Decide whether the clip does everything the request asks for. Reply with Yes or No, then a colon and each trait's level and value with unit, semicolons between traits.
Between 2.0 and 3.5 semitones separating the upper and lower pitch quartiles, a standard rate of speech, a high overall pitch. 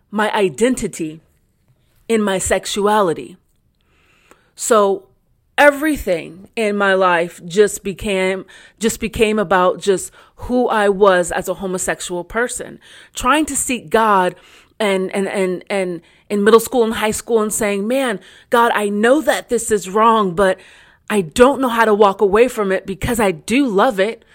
Yes: average, 3.2 semitones; average, 155 wpm; high, 205 Hz